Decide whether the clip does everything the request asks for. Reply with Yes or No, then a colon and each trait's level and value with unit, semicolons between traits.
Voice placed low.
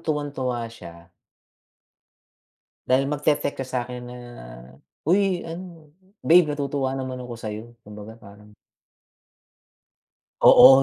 Yes: low, 130 Hz